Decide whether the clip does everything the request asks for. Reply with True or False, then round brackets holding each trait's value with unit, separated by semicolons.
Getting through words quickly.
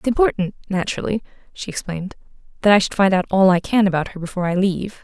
True (215 wpm)